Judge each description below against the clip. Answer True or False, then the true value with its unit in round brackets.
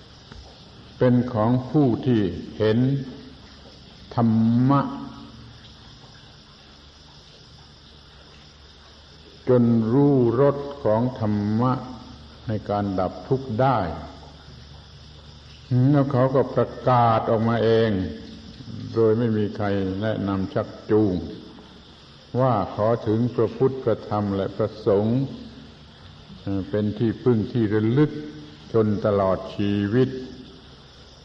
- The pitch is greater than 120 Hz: False (105 Hz)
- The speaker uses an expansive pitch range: True (7.9 semitones)